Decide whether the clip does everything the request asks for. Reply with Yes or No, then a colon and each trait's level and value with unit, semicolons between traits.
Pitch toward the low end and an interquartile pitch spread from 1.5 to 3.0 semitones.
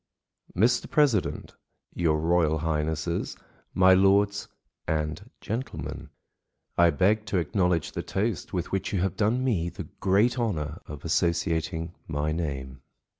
No: very low, 85 Hz; average, 4.2 semitones